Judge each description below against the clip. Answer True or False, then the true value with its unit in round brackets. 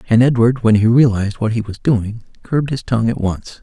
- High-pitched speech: False (115 Hz)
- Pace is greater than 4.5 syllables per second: True (5.9 syllables/s)